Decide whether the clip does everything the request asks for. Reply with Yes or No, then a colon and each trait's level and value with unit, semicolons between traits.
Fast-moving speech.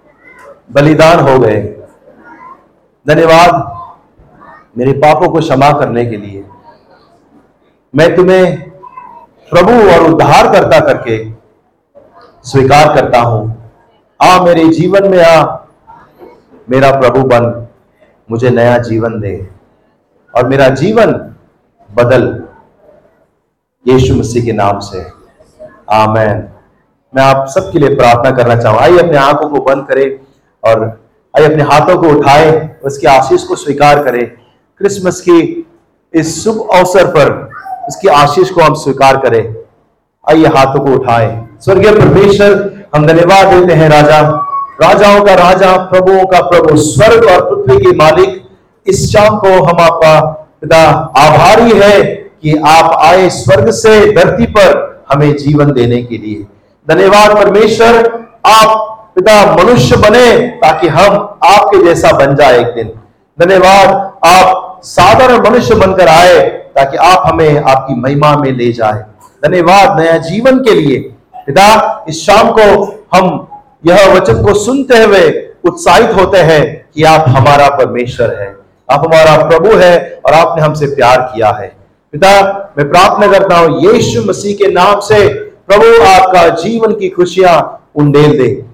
No: average, 135 wpm